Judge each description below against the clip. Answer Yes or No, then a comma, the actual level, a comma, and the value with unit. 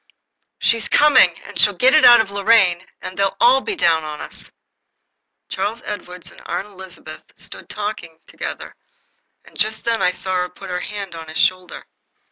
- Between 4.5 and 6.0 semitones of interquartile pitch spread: No, average, 3.7 semitones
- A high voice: Yes, high, 195 Hz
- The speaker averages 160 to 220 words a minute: Yes, average, 175 wpm